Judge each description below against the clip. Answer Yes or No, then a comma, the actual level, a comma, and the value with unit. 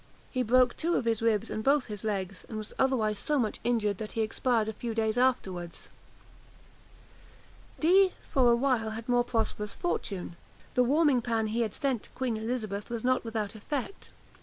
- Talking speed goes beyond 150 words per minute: Yes, average, 185 wpm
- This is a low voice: No, high, 230 Hz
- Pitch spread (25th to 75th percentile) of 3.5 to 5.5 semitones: No, average, 2.9 semitones